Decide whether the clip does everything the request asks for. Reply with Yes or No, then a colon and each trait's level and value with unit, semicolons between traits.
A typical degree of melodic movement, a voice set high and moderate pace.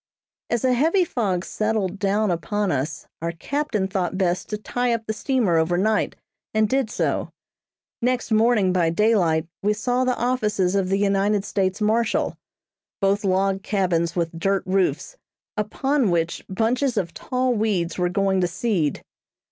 Yes: average, 3.8 semitones; high, 200 Hz; average, 155 wpm